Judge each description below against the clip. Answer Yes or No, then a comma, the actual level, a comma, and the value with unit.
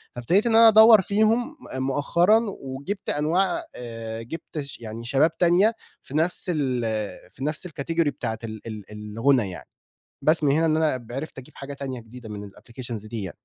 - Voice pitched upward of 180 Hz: No, medium, 140 Hz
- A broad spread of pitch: Yes, wide, 6.7 semitones